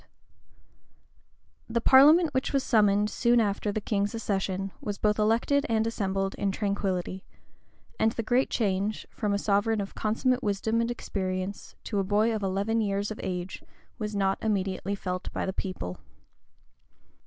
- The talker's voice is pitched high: Yes, high, 205 Hz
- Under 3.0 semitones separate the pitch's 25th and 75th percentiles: Yes, narrow, 2.4 semitones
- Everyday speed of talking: Yes, average, 155 wpm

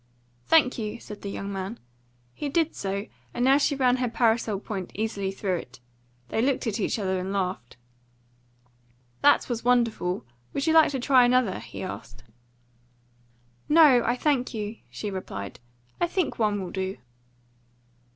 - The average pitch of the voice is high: Yes, high, 225 Hz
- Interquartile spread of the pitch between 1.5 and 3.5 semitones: No, average, 4.7 semitones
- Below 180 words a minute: Yes, average, 160 wpm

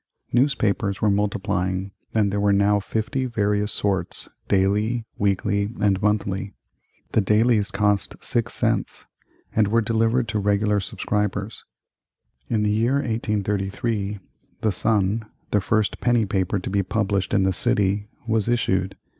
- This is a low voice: Yes, low, 105 Hz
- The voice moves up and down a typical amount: No, narrow, 2.0 semitones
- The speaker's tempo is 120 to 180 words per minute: Yes, slow, 135 wpm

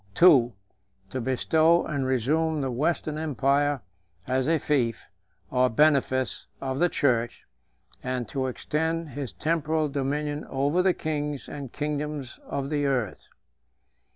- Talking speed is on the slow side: Yes, slow, 130 wpm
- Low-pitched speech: No, medium, 145 Hz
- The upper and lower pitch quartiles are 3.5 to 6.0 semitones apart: No, average, 2.8 semitones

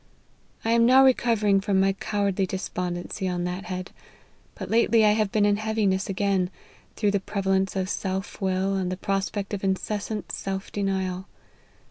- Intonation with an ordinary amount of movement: No, narrow, 1.7 semitones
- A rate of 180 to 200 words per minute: No, average, 165 wpm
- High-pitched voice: Yes, high, 195 Hz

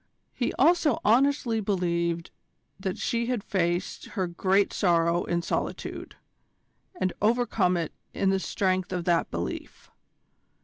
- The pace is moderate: No, slow, 125 wpm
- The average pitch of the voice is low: No, medium, 185 Hz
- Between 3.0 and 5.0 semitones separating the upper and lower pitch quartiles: Yes, average, 4.3 semitones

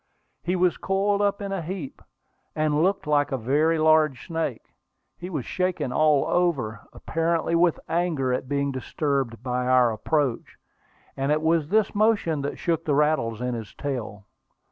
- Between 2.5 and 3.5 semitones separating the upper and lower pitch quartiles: No, average, 4.6 semitones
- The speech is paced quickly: No, average, 165 wpm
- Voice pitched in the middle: Yes, medium, 155 Hz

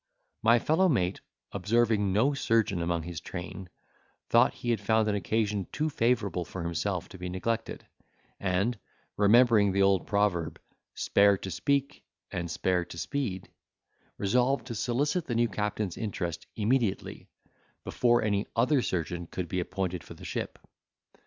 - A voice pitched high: No, low, 105 Hz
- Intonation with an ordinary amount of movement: Yes, average, 4.4 semitones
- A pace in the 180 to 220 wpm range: No, average, 145 wpm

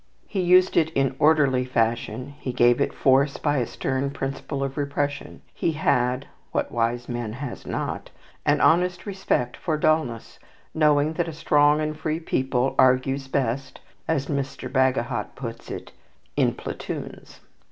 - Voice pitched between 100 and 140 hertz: Yes, low, 135 Hz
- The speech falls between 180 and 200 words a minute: No, average, 150 wpm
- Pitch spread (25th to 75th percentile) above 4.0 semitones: No, average, 3.2 semitones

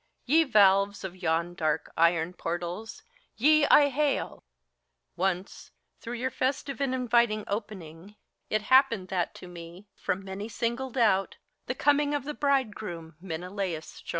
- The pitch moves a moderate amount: No, wide, 6.6 semitones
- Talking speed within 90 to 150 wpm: Yes, average, 140 wpm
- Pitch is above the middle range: Yes, high, 205 Hz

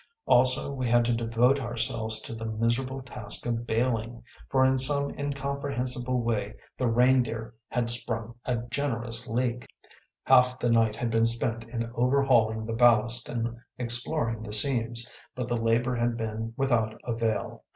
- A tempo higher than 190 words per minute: No, average, 150 wpm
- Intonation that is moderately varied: No, narrow, 1.9 semitones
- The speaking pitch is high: No, low, 120 Hz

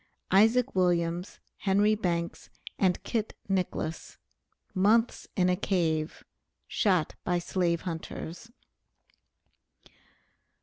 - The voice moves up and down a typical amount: Yes, average, 3.3 semitones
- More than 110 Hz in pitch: Yes, medium, 185 Hz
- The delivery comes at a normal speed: No, slow, 85 wpm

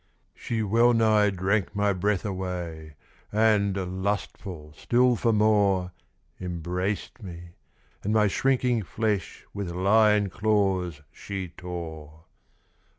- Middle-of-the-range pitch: No, low, 100 Hz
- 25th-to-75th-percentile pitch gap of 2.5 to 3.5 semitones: Yes, average, 3.0 semitones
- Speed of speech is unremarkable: No, slow, 105 wpm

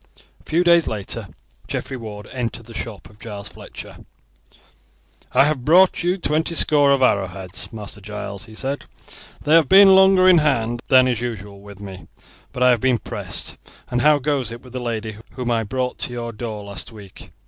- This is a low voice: Yes, low, 120 Hz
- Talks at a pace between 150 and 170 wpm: No, average, 190 wpm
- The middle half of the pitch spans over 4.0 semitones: Yes, wide, 5.5 semitones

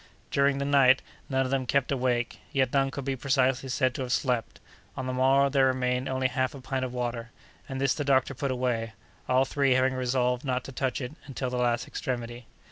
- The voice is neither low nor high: No, low, 130 Hz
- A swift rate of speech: Yes, fast, 215 wpm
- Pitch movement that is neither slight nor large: No, narrow, 1.4 semitones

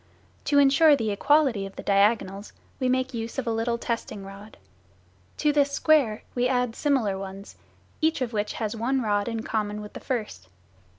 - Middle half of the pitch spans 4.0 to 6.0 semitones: Yes, average, 4.3 semitones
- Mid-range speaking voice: No, high, 230 Hz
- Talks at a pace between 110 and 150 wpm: No, average, 180 wpm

